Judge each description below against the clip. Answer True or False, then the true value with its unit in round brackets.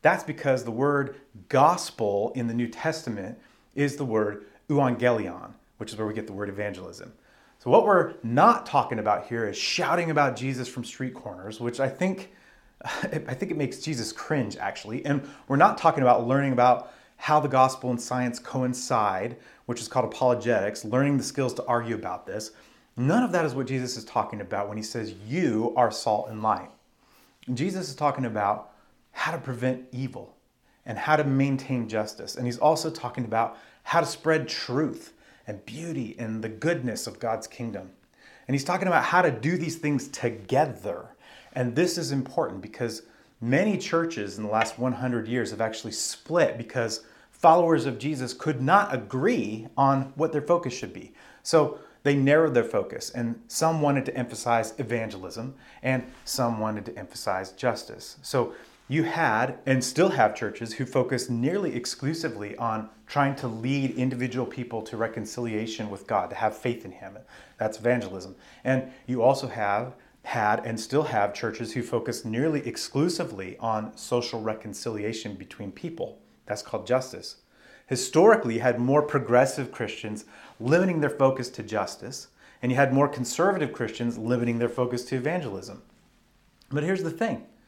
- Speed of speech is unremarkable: True (170 wpm)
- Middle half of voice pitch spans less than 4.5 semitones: True (3.7 semitones)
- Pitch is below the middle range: True (125 Hz)